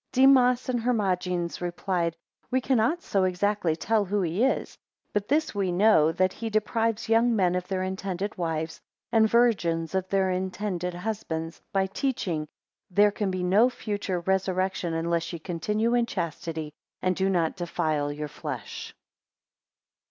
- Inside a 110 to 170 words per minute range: Yes, average, 150 wpm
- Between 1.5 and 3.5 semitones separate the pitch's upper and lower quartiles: No, average, 4.0 semitones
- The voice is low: No, high, 190 Hz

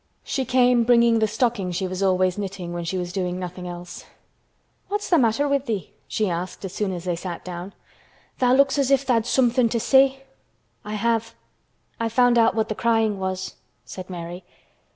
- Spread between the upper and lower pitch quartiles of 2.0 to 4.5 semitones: No, average, 5.0 semitones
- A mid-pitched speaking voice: No, high, 215 Hz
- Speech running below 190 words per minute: No, average, 195 wpm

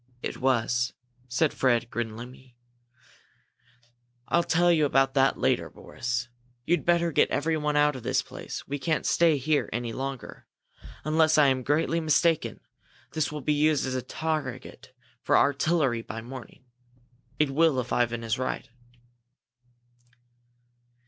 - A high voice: No, low, 135 Hz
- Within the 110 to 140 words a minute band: Yes, slow, 135 wpm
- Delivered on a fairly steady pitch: No, average, 3.9 semitones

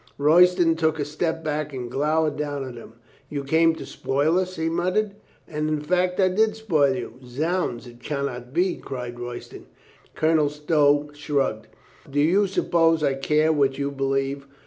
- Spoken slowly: No, average, 170 wpm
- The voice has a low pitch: No, medium, 150 Hz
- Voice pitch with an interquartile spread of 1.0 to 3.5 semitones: Yes, average, 3.1 semitones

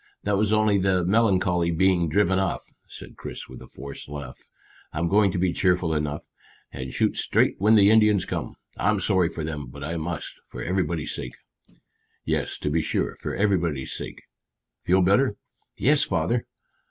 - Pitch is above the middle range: No, very low, 90 Hz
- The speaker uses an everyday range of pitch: Yes, average, 4.1 semitones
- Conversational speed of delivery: Yes, average, 170 wpm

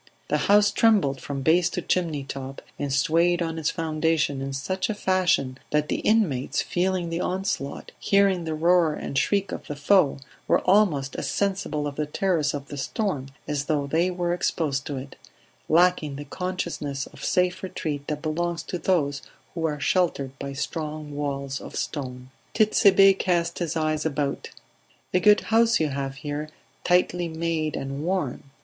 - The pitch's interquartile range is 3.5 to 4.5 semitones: Yes, average, 4.2 semitones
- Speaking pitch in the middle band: Yes, medium, 160 Hz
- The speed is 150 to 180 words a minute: Yes, average, 170 wpm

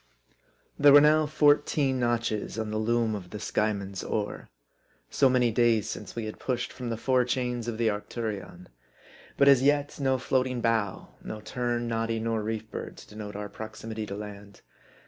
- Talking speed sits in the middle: Yes, average, 175 wpm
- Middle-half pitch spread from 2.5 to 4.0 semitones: Yes, average, 3.0 semitones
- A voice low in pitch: Yes, low, 115 Hz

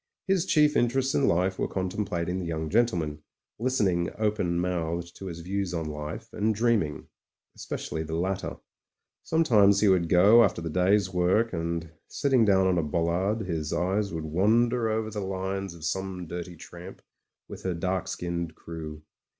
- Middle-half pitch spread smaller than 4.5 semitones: Yes, average, 3.9 semitones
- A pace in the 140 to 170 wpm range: Yes, average, 165 wpm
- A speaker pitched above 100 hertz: No, very low, 95 Hz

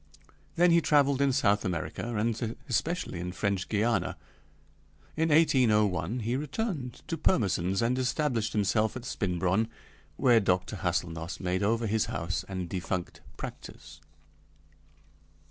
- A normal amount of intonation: No, wide, 5.7 semitones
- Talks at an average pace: No, slow, 125 wpm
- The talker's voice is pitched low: Yes, low, 110 Hz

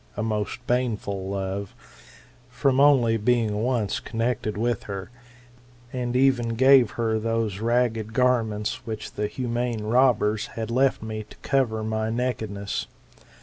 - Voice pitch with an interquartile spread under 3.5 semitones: Yes, average, 2.7 semitones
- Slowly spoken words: Yes, slow, 130 wpm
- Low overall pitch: Yes, low, 115 Hz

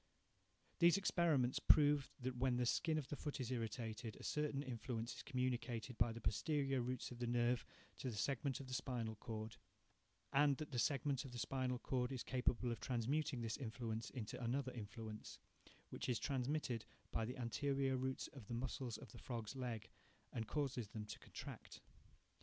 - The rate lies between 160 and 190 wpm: Yes, average, 180 wpm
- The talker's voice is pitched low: Yes, low, 125 Hz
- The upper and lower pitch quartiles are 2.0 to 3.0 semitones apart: Yes, average, 2.7 semitones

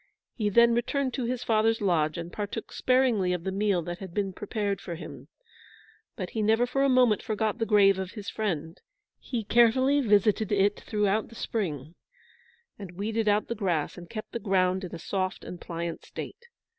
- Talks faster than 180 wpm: Yes, average, 190 wpm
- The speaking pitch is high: Yes, high, 205 Hz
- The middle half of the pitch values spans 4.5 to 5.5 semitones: No, average, 3.6 semitones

